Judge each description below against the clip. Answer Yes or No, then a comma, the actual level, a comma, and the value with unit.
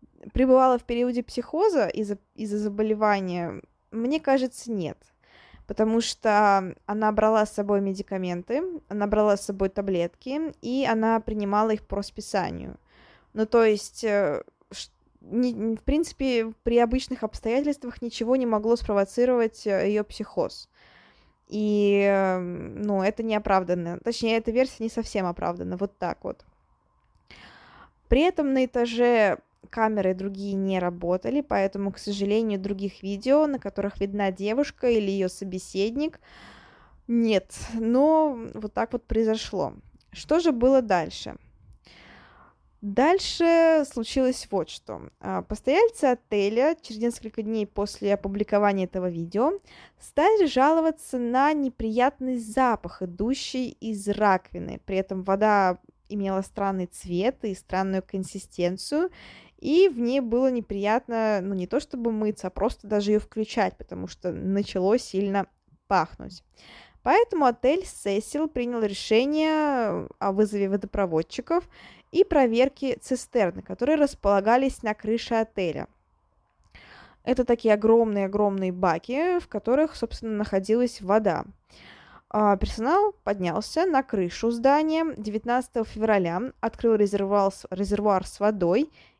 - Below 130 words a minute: Yes, average, 115 wpm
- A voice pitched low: No, high, 220 Hz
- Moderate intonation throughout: Yes, average, 4.1 semitones